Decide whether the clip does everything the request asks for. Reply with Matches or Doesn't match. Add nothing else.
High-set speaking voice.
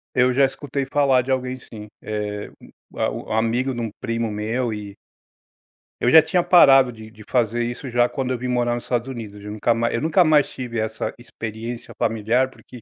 Doesn't match